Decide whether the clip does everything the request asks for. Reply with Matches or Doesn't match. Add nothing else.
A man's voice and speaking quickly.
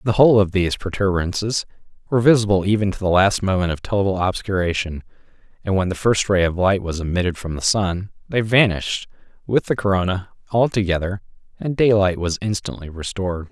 Doesn't match